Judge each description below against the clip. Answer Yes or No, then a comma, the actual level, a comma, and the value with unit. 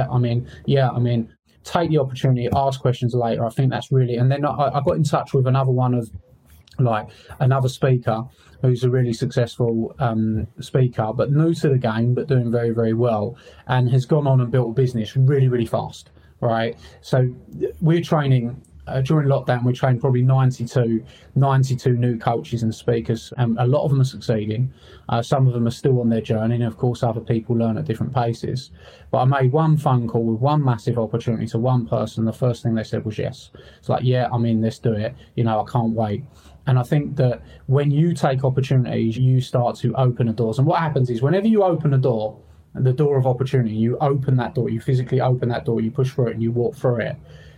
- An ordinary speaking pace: No, fast, 220 wpm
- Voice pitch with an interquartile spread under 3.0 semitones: Yes, narrow, 2.5 semitones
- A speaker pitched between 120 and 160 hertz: Yes, low, 125 Hz